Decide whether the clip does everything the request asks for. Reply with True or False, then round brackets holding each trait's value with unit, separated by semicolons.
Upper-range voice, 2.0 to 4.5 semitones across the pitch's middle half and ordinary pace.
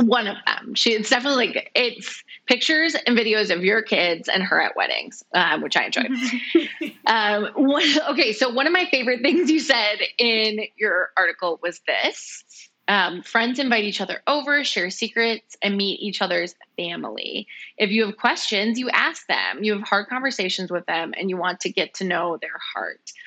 False (225 Hz; 5.0 semitones; 190 wpm)